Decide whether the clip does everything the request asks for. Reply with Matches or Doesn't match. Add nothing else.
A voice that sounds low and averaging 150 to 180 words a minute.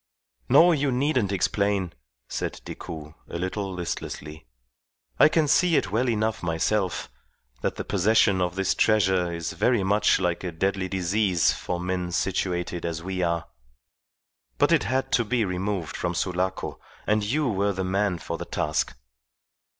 Matches